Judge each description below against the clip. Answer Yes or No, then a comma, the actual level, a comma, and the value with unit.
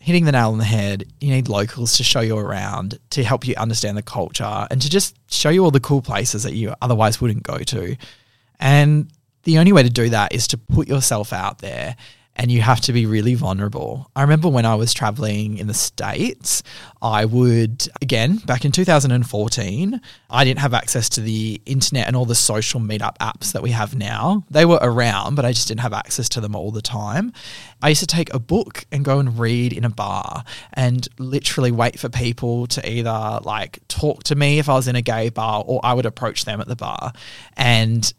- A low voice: Yes, low, 120 Hz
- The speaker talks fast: Yes, fast, 220 wpm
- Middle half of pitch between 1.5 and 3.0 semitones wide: No, average, 3.6 semitones